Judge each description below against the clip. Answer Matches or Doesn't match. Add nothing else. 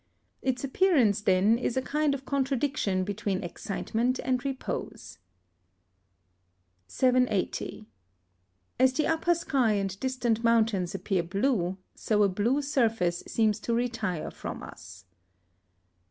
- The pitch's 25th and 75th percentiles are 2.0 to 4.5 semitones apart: Doesn't match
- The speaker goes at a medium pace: Doesn't match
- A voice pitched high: Matches